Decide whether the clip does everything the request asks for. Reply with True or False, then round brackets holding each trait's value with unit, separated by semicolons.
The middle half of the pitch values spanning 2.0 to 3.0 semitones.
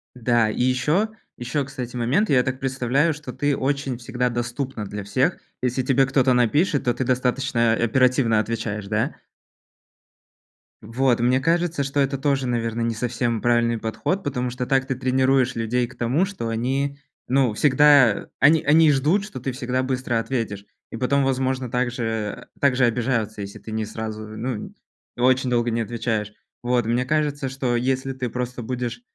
True (2.4 semitones)